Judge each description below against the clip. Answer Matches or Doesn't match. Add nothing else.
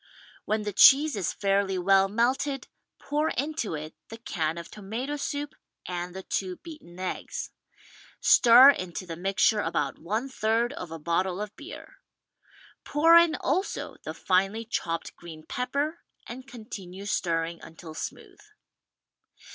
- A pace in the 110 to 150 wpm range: Matches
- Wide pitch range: Matches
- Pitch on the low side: Doesn't match